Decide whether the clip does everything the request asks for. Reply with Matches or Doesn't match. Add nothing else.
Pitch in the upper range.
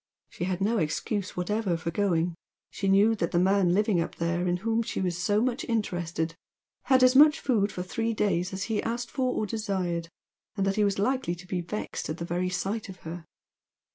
Matches